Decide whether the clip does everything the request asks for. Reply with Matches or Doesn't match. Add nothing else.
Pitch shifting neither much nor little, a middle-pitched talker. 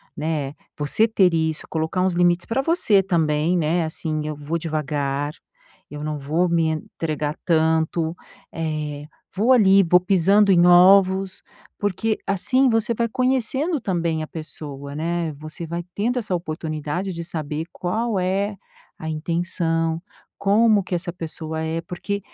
Matches